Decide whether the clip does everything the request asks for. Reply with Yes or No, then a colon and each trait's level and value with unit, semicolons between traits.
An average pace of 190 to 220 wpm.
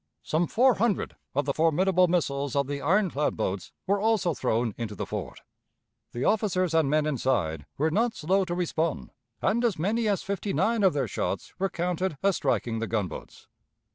No: average, 180 wpm